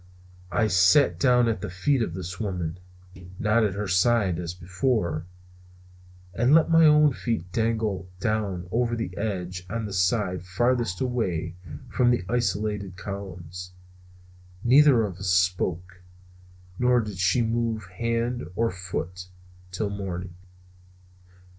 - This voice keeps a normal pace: No, slow, 130 wpm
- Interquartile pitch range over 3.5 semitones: Yes, average, 4.4 semitones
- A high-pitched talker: No, low, 100 Hz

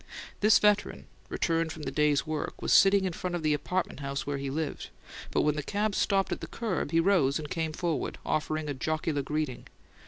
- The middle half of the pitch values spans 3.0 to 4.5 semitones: Yes, average, 3.7 semitones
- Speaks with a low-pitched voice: No, medium, 155 Hz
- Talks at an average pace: No, fast, 210 wpm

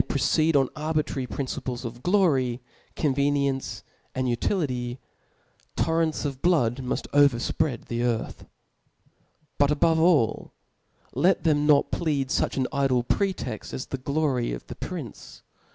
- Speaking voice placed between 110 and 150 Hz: Yes, medium, 140 Hz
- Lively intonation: No, average, 3.7 semitones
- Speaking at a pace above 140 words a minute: No, slow, 135 wpm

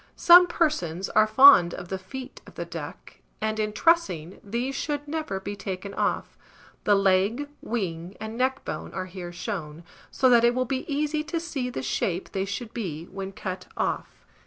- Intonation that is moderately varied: No, wide, 6.0 semitones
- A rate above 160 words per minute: Yes, average, 180 wpm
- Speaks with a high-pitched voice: Yes, high, 215 Hz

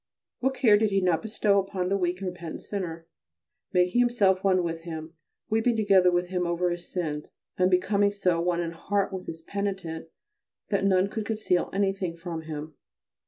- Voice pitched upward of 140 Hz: Yes, medium, 185 Hz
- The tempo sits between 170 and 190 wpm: Yes, average, 180 wpm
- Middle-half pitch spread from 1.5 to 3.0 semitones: Yes, average, 2.7 semitones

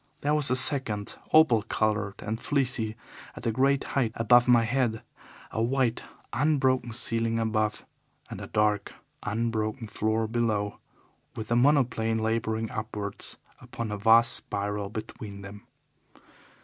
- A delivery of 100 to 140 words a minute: Yes, slow, 135 wpm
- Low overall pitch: Yes, low, 115 Hz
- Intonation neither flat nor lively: No, narrow, 2.3 semitones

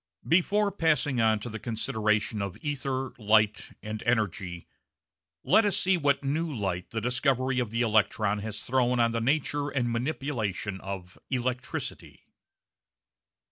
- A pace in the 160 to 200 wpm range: No, average, 140 wpm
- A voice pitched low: Yes, low, 120 Hz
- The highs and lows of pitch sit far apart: No, average, 4.5 semitones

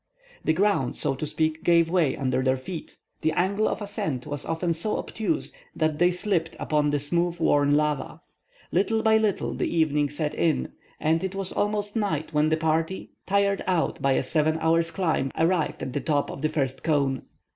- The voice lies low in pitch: No, medium, 160 Hz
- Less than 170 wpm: No, average, 190 wpm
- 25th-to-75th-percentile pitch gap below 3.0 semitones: No, average, 3.9 semitones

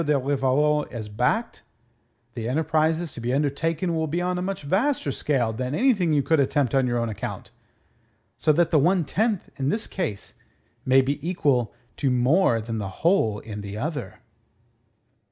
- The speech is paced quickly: No, average, 170 wpm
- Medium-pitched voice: Yes, medium, 145 Hz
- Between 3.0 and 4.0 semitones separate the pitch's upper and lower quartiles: No, average, 5.2 semitones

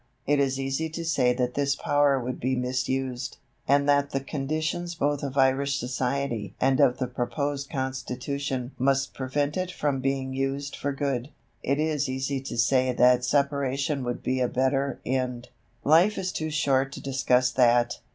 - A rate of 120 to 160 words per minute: No, average, 170 wpm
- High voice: No, low, 135 Hz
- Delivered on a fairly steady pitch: Yes, narrow, 1.8 semitones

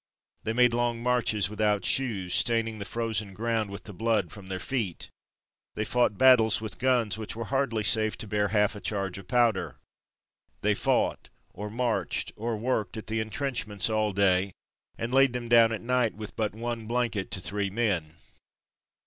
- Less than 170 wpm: No, average, 175 wpm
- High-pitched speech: No, low, 110 Hz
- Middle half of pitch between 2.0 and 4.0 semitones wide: Yes, narrow, 2.6 semitones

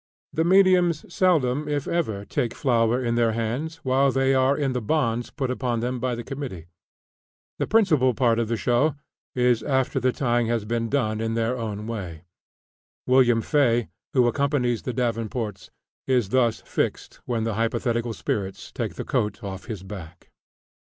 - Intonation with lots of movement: No, average, 2.9 semitones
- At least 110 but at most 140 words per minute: No, average, 165 wpm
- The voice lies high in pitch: No, low, 120 Hz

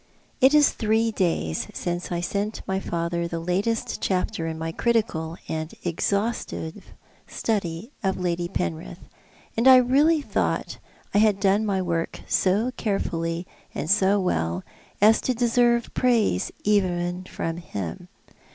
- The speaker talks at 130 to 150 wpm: Yes, slow, 135 wpm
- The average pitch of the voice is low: No, high, 190 Hz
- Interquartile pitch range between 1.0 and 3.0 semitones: No, average, 4.8 semitones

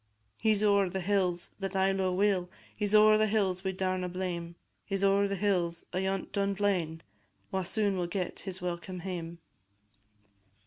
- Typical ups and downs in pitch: No, narrow, 1.9 semitones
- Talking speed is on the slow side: No, average, 175 wpm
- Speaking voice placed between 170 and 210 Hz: Yes, high, 190 Hz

